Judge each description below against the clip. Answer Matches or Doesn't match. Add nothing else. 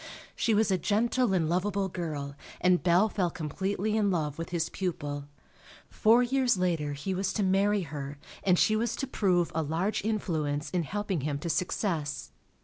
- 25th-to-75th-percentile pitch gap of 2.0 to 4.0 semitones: Doesn't match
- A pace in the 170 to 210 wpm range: Matches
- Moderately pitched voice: Matches